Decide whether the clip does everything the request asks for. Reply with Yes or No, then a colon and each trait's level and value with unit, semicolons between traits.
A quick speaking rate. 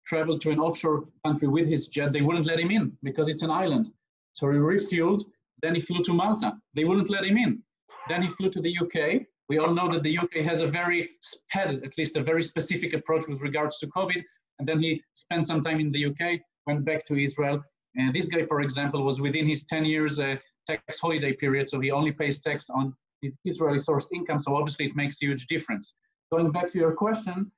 Yes: fast, 230 wpm